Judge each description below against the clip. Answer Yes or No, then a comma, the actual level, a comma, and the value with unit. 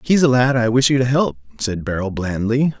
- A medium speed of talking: No, fast, 255 wpm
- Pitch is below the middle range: Yes, low, 120 Hz